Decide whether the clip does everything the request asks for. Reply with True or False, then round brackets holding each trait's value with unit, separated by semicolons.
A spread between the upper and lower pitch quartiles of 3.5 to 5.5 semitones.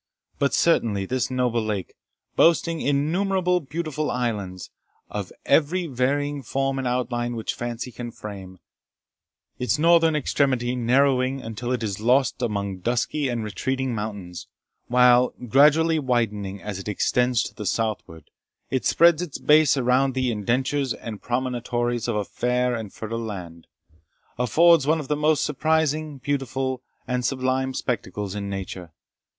True (4.1 semitones)